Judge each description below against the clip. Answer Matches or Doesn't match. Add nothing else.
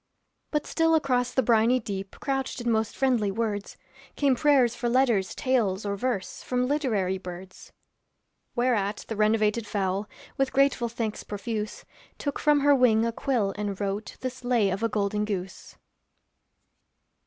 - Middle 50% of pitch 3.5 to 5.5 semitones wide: Matches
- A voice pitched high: Matches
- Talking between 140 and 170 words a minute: Matches